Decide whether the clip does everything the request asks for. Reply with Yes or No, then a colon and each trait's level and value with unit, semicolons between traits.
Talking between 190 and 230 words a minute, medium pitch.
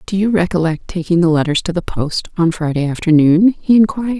Yes: average, 200 wpm; medium, 175 Hz